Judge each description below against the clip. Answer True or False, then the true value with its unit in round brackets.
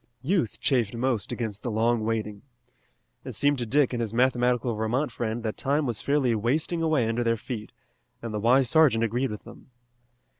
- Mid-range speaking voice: False (120 Hz)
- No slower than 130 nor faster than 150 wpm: False (185 wpm)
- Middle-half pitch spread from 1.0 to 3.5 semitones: True (2.9 semitones)